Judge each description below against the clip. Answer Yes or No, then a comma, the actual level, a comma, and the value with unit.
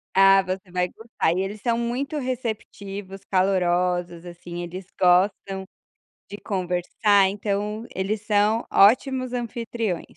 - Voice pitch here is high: Yes, high, 195 Hz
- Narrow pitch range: No, average, 3.5 semitones